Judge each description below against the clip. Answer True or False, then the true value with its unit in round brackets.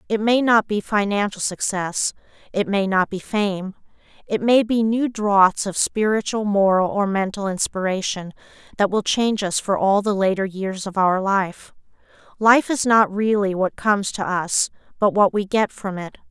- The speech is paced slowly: False (175 wpm)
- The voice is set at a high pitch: True (200 Hz)